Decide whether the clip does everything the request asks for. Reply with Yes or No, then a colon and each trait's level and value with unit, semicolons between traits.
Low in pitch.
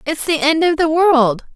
No: very high, 305 Hz